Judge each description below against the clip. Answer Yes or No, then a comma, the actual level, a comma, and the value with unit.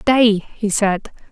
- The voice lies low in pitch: No, high, 210 Hz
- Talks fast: No, slow, 135 wpm